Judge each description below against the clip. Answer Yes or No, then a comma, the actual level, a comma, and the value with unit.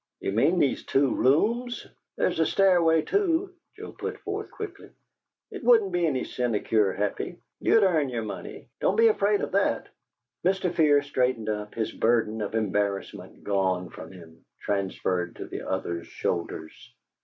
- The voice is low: Yes, low, 130 Hz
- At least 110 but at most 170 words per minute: Yes, average, 155 wpm